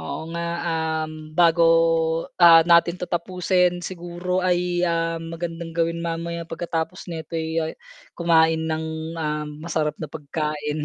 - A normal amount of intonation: No, narrow, 1.3 semitones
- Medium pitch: Yes, medium, 165 Hz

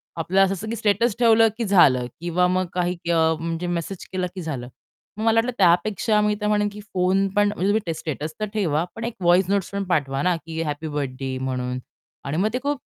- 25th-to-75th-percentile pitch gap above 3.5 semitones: Yes, average, 4.5 semitones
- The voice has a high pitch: No, medium, 180 Hz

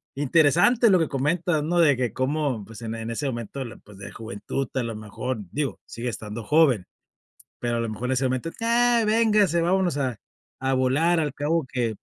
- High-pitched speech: No, low, 135 Hz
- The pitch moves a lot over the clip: Yes, wide, 6.0 semitones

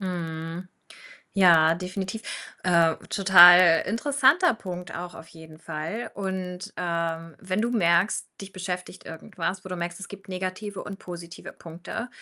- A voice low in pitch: No, medium, 180 Hz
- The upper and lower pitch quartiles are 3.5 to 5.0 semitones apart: No, narrow, 2.5 semitones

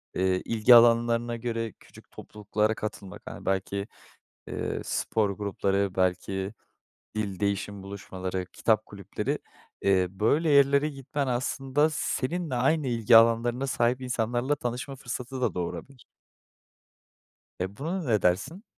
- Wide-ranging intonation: No, average, 4.7 semitones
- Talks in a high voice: No, low, 115 Hz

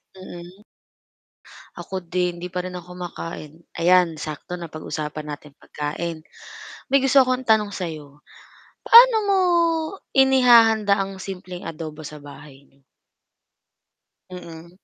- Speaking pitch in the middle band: Yes, medium, 180 Hz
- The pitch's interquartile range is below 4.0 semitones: No, average, 4.3 semitones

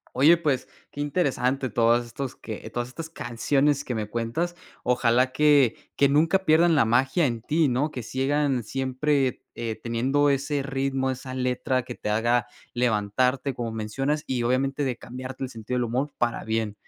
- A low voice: Yes, low, 130 Hz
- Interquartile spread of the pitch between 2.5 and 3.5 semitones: Yes, average, 3.1 semitones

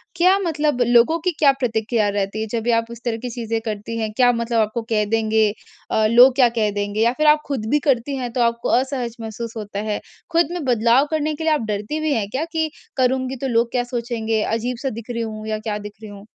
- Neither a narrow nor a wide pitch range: Yes, average, 3.3 semitones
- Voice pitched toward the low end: No, high, 235 Hz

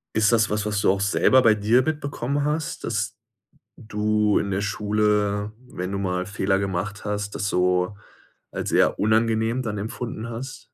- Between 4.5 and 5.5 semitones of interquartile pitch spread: No, narrow, 2.4 semitones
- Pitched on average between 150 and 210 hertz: No, low, 105 Hz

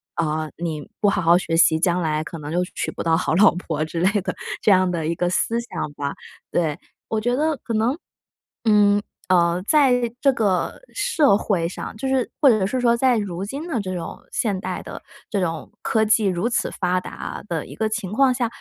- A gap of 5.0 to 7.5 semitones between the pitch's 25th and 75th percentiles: Yes, wide, 5.5 semitones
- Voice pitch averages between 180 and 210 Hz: Yes, high, 195 Hz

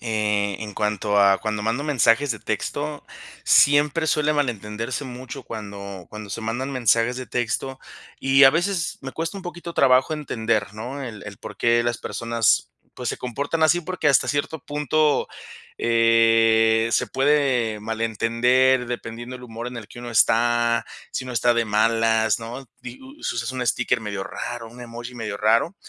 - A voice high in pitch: No, low, 120 Hz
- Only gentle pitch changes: No, average, 3.1 semitones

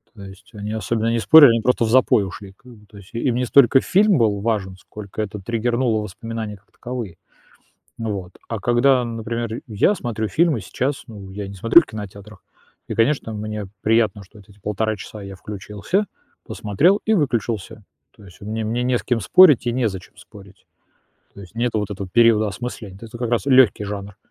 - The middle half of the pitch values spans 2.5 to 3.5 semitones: Yes, average, 3.0 semitones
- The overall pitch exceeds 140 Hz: No, low, 110 Hz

